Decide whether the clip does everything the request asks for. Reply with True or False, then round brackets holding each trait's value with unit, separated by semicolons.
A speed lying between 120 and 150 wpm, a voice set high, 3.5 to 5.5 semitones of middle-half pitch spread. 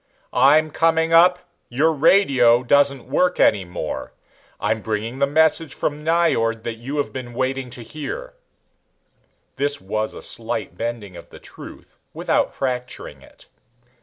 False (140 wpm; 135 Hz; 5.2 semitones)